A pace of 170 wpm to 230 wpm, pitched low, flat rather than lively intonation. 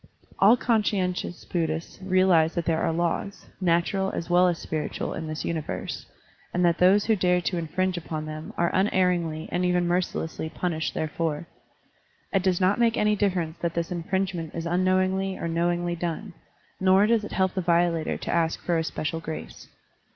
No: average, 175 wpm; medium, 175 Hz; narrow, 2.2 semitones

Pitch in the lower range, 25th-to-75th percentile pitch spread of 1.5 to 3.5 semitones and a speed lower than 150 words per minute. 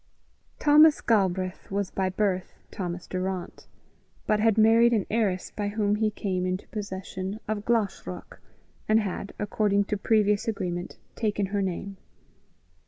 No: high, 205 Hz; narrow, 2.4 semitones; slow, 135 wpm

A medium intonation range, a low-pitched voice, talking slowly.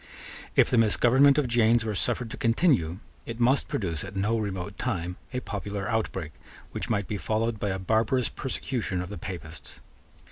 No: average, 3.9 semitones; low, 110 Hz; average, 175 wpm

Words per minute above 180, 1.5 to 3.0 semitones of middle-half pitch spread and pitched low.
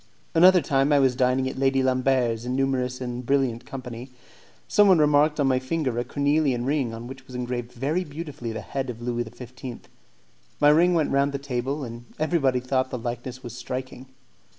Yes: average, 190 wpm; narrow, 2.4 semitones; low, 130 Hz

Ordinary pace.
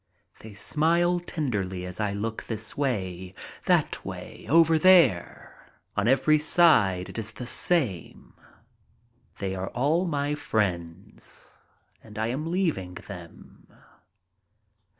No: slow, 120 wpm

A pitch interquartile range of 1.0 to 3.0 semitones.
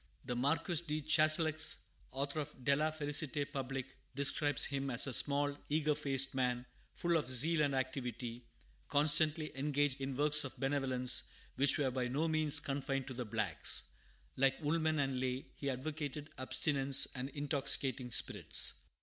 Yes: narrow, 2.4 semitones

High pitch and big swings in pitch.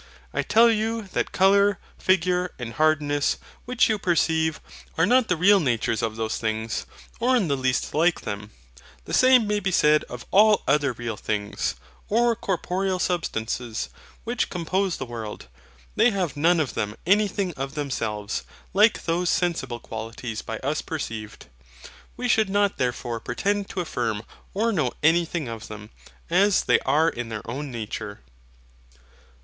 No: medium, 160 Hz; wide, 8.8 semitones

